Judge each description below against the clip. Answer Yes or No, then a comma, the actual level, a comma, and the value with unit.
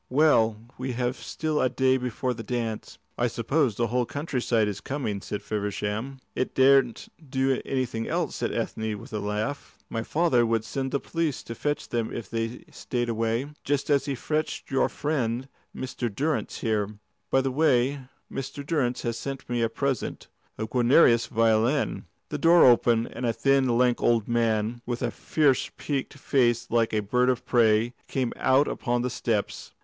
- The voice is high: No, low, 125 Hz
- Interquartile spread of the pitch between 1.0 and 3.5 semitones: Yes, average, 3.1 semitones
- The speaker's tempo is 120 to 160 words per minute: No, average, 175 wpm